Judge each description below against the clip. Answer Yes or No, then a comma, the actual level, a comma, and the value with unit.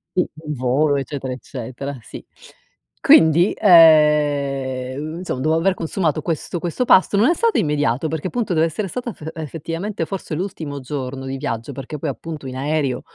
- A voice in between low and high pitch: Yes, medium, 150 Hz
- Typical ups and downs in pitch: Yes, average, 3.7 semitones